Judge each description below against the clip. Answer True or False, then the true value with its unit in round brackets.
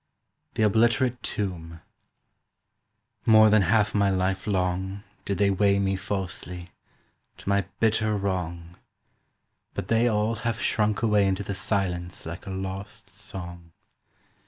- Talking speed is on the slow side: True (130 wpm)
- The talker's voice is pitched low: True (100 Hz)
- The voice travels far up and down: False (2.4 semitones)